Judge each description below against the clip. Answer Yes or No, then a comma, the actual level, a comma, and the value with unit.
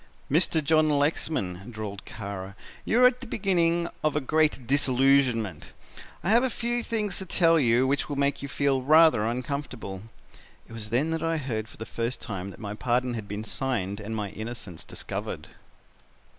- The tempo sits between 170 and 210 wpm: Yes, average, 180 wpm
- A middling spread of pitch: No, wide, 6.5 semitones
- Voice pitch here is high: No, low, 130 Hz